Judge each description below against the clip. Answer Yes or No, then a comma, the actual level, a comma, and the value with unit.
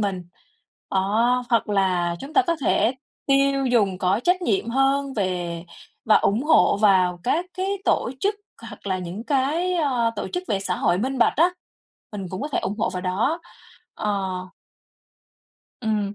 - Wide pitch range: Yes, wide, 6.2 semitones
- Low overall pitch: No, high, 220 Hz